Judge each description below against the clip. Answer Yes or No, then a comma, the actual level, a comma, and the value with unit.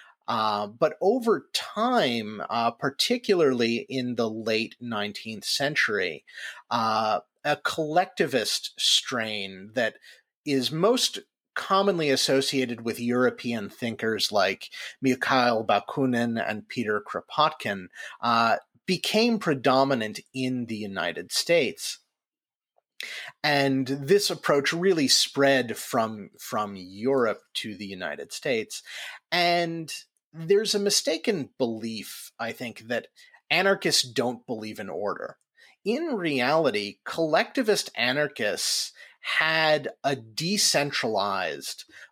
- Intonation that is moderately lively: No, wide, 7.5 semitones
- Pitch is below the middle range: Yes, low, 130 Hz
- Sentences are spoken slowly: Yes, slow, 95 wpm